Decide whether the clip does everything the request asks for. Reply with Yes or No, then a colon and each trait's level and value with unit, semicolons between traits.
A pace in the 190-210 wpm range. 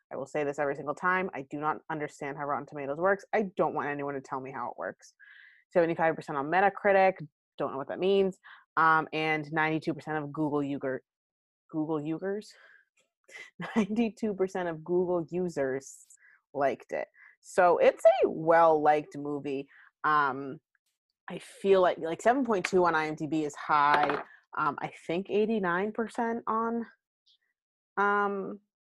No: average, 155 wpm